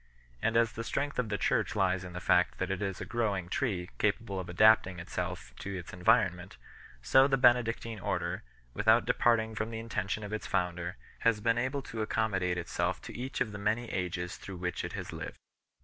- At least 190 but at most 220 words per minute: Yes, average, 200 wpm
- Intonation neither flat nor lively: Yes, average, 4.0 semitones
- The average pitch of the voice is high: No, low, 105 Hz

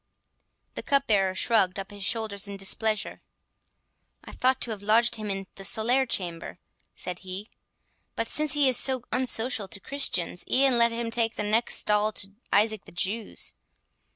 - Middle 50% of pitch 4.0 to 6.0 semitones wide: No, average, 3.3 semitones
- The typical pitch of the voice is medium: No, high, 220 Hz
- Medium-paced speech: Yes, average, 165 wpm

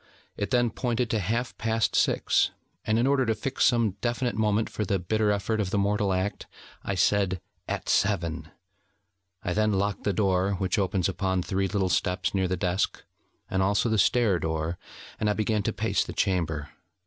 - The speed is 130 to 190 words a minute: Yes, average, 185 wpm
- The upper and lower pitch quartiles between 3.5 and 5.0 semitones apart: No, average, 3.0 semitones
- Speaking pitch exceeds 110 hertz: No, low, 100 Hz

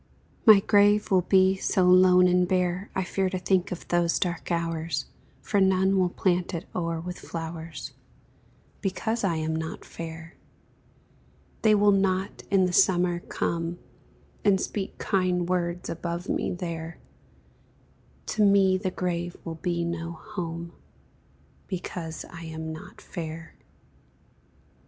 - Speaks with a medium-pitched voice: Yes, medium, 180 Hz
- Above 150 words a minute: No, slow, 135 wpm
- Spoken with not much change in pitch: Yes, narrow, 2.1 semitones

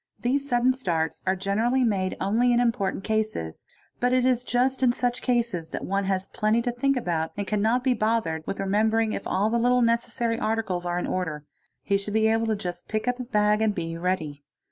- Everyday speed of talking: No, fast, 210 wpm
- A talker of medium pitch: No, high, 220 Hz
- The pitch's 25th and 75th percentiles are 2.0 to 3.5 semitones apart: No, average, 4.3 semitones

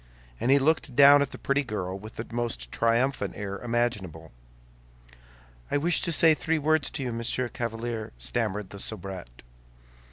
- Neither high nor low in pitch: No, low, 120 Hz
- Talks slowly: No, average, 160 wpm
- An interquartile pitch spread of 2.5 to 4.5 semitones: No, wide, 5.5 semitones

